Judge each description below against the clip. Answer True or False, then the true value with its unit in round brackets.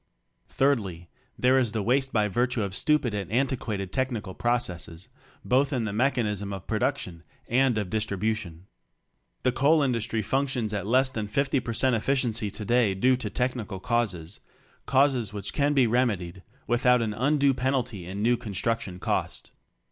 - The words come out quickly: False (165 wpm)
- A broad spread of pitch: False (4.2 semitones)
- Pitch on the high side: False (115 Hz)